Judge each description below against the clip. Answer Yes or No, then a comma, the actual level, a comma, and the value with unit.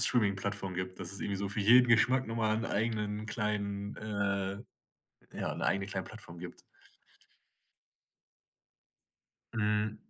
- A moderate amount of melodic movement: No, narrow, 1.8 semitones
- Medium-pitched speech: No, low, 105 Hz